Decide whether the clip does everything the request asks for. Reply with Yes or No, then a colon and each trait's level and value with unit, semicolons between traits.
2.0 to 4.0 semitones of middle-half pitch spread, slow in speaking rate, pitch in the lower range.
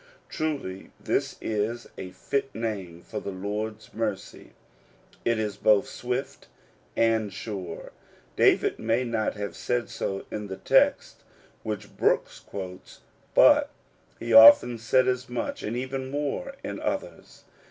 Yes: average, 3.3 semitones; slow, 130 wpm; low, 110 Hz